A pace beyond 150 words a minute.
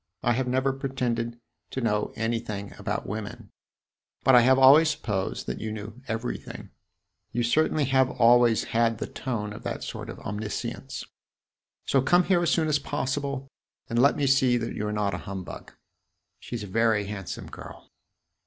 Yes: average, 170 wpm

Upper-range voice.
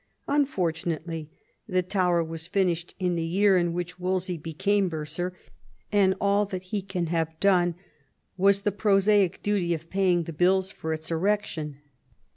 No: medium, 180 Hz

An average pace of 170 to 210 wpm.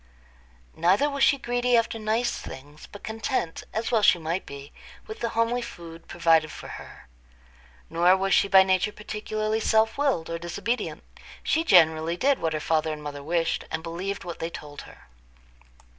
Yes: average, 175 wpm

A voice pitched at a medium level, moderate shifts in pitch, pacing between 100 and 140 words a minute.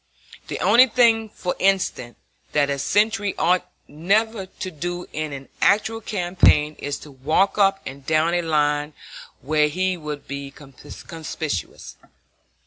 Yes: medium, 165 Hz; average, 4.9 semitones; slow, 135 wpm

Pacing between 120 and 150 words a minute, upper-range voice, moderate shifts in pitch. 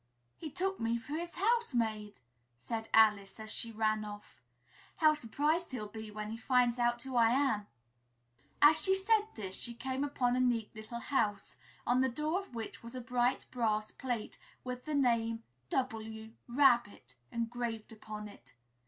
No: average, 165 wpm; high, 235 Hz; average, 3.4 semitones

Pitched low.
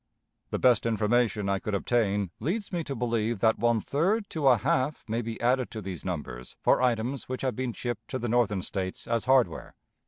Yes: low, 120 Hz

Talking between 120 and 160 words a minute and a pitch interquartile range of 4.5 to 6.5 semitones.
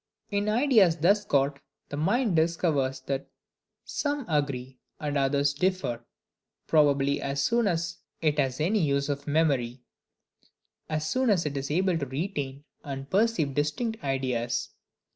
Yes: average, 140 wpm; average, 5.1 semitones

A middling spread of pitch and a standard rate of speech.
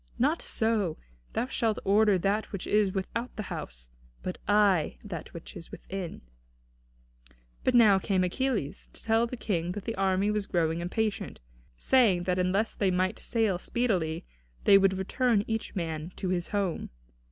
Yes: average, 3.4 semitones; average, 160 wpm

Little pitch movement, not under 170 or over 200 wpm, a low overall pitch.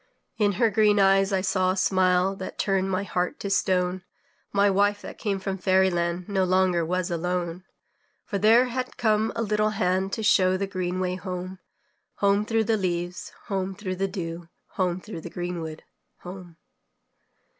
No: narrow, 1.9 semitones; average, 175 wpm; high, 190 Hz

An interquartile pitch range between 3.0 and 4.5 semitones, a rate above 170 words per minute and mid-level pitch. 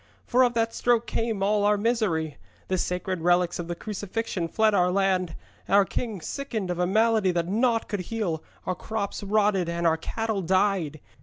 No: average, 3.8 semitones; average, 180 wpm; high, 195 Hz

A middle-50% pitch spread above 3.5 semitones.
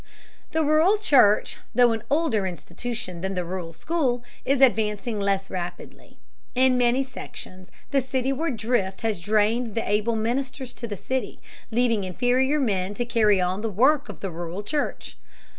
Yes: average, 5.0 semitones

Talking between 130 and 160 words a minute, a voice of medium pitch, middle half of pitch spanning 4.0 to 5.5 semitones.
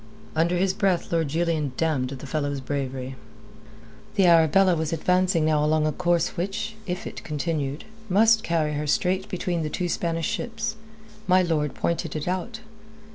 No: average, 155 wpm; medium, 165 Hz; average, 3.3 semitones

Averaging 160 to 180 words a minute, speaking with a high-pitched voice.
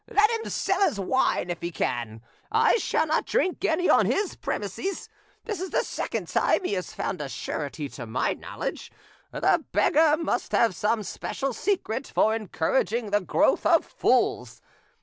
Yes: average, 170 wpm; high, 225 Hz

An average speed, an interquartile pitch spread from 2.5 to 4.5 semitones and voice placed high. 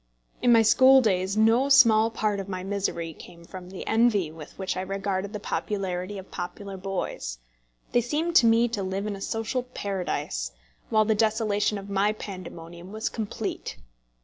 Yes: average, 175 wpm; average, 3.0 semitones; high, 200 Hz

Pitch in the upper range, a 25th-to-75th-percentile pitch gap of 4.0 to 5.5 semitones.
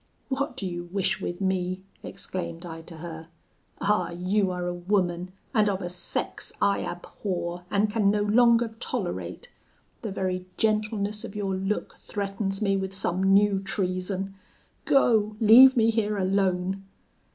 No: high, 195 Hz; average, 2.7 semitones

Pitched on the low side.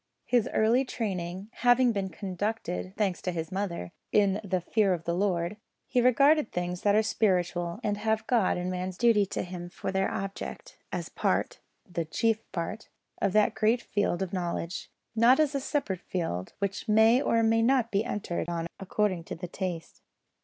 No: high, 200 Hz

